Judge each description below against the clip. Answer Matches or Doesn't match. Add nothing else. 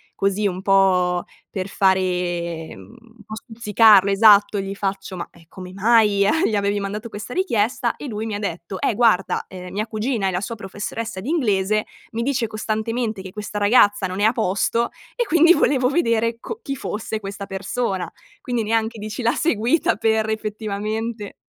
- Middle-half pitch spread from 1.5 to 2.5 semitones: Doesn't match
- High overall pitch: Matches